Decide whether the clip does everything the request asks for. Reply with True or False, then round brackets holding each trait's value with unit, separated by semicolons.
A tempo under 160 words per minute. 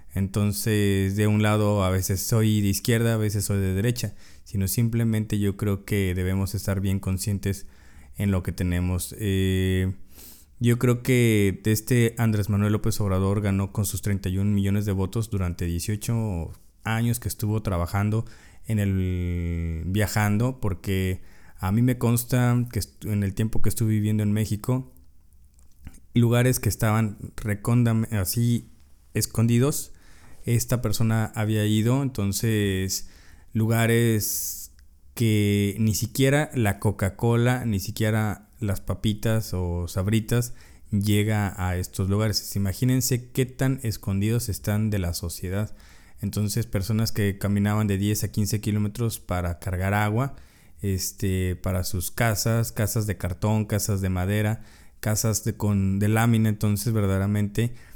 True (135 wpm)